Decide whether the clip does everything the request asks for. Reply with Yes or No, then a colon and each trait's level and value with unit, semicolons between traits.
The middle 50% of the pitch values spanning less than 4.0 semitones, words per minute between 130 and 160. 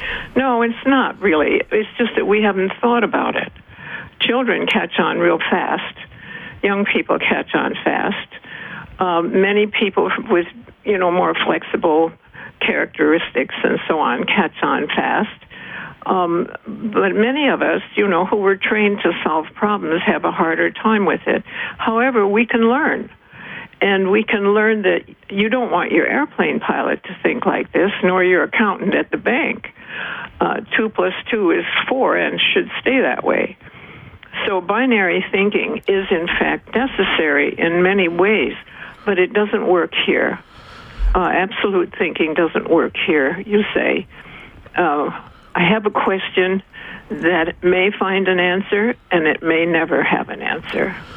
Yes: average, 3.5 semitones; average, 155 wpm